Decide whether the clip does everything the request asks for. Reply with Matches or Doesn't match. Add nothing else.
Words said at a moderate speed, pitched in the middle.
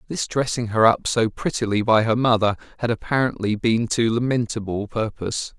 Doesn't match